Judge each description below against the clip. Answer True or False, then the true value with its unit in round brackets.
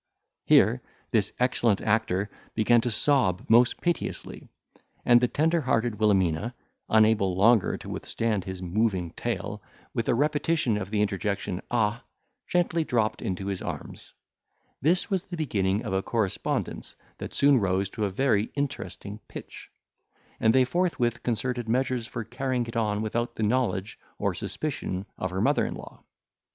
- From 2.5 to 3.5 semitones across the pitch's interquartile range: False (4.1 semitones)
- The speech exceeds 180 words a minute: False (150 wpm)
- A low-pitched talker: True (115 Hz)